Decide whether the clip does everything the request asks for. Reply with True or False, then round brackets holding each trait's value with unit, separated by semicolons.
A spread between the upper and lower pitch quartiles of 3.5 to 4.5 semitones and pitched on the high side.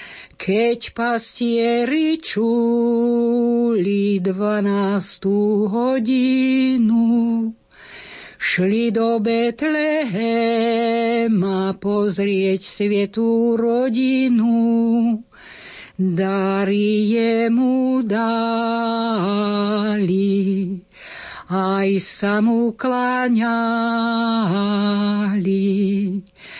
False (2.7 semitones; 230 Hz)